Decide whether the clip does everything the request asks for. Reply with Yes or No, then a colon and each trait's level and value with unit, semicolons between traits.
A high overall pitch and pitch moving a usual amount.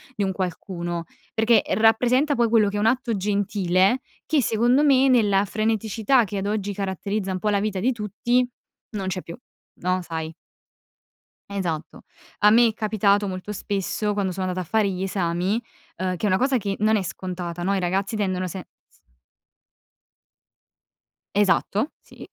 Yes: high, 200 Hz; average, 3.0 semitones